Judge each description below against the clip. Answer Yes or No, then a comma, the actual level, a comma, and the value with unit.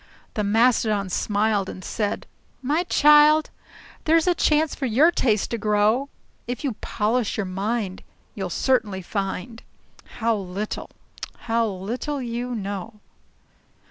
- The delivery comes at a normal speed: No, slow, 125 wpm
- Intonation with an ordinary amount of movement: Yes, average, 3.9 semitones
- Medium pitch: No, high, 225 Hz